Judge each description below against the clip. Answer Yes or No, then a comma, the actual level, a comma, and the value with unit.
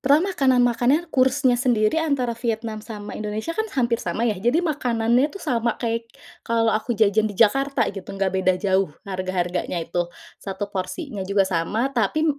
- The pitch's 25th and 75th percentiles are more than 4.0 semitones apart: Yes, average, 4.5 semitones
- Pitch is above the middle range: Yes, high, 230 Hz